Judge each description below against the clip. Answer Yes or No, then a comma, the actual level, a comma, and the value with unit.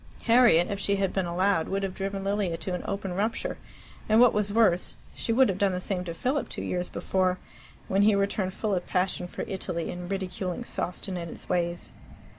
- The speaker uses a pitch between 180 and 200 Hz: Yes, high, 190 Hz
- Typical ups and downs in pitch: No, narrow, 2.0 semitones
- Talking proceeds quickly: Yes, fast, 210 wpm